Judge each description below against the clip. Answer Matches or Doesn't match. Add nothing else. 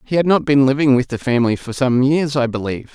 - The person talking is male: Matches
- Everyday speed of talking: Doesn't match